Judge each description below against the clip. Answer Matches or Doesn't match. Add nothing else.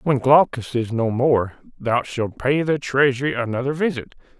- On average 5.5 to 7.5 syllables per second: Doesn't match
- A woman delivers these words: Doesn't match